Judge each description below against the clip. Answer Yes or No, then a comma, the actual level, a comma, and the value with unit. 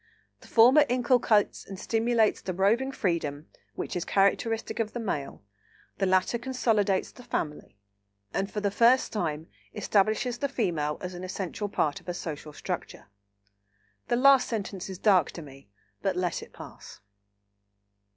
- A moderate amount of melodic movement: Yes, average, 4.8 semitones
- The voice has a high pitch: Yes, high, 200 Hz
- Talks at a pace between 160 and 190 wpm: No, average, 150 wpm